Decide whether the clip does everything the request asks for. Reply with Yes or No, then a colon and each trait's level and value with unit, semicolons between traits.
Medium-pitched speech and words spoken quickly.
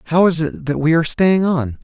Yes: medium, 145 Hz; fast, 260 wpm